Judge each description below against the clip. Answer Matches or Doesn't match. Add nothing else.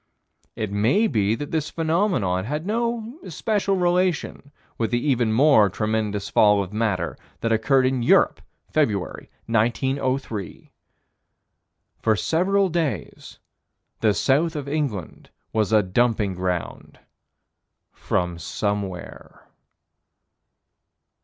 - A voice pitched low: Matches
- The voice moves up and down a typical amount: Doesn't match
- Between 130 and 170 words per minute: Doesn't match